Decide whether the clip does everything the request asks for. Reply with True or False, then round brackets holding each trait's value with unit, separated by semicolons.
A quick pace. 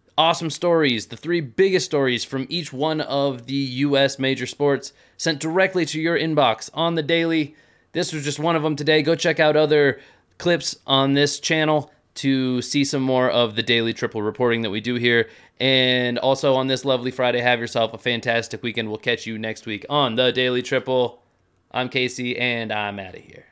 False (195 wpm)